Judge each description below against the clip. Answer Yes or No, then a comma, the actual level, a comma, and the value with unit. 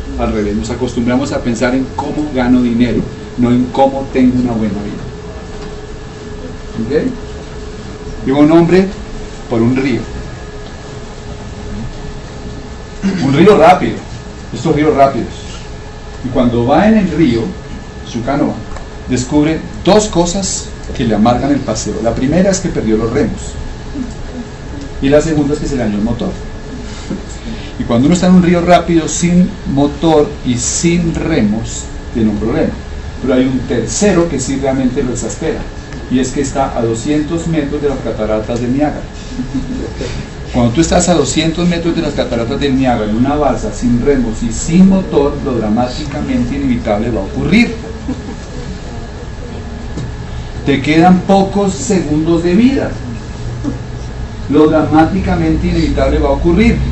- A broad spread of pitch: Yes, wide, 5.8 semitones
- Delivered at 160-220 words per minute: No, average, 145 wpm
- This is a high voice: No, low, 135 Hz